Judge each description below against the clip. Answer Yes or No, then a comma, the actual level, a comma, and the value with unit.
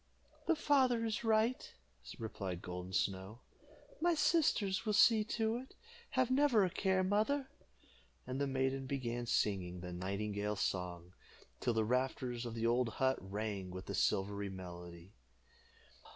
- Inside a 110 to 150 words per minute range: Yes, average, 140 wpm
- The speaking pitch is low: Yes, low, 120 Hz